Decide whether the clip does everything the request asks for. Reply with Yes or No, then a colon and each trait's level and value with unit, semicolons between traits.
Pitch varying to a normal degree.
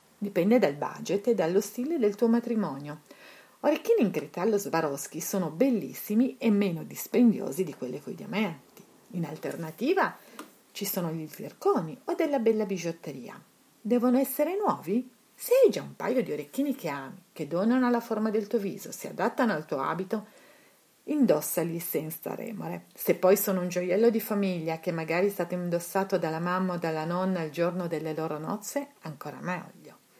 No: wide, 5.8 semitones